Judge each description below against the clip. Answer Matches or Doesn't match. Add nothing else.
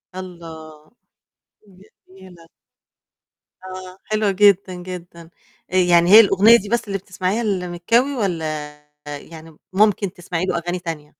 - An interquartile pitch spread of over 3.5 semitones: Doesn't match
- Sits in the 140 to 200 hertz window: Matches